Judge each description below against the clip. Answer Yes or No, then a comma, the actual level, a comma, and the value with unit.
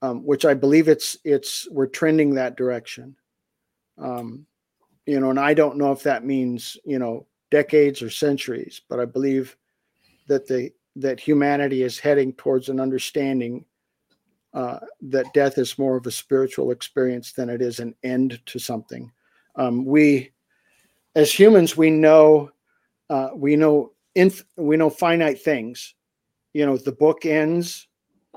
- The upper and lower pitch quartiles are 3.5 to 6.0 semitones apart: No, average, 2.9 semitones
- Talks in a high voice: No, low, 135 Hz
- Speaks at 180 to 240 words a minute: No, average, 150 wpm